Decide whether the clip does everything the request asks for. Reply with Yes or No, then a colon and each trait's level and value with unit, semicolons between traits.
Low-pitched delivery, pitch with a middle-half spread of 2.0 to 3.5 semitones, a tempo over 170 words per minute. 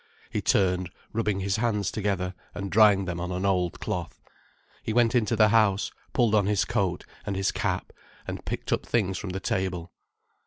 Yes: low, 100 Hz; narrow, 2.6 semitones; average, 190 wpm